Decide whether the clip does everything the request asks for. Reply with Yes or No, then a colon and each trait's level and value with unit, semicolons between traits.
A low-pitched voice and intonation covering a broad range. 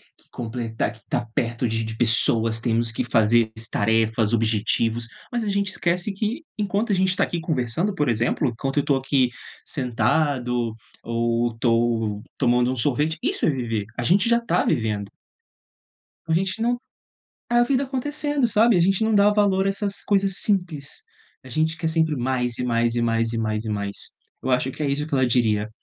Yes: low, 130 Hz; wide, 8.6 semitones